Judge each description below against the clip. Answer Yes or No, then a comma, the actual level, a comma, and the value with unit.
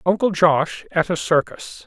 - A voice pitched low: No, medium, 170 Hz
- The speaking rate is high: No, average, 160 wpm